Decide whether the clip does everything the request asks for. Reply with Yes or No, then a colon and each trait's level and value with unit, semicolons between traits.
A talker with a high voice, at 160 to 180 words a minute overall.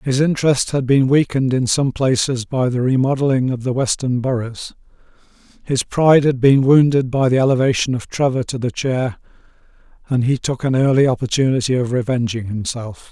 No: low, 130 Hz; average, 170 wpm